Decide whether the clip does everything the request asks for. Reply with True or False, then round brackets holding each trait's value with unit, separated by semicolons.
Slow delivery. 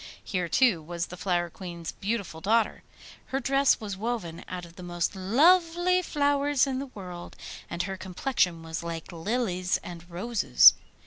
False (155 wpm)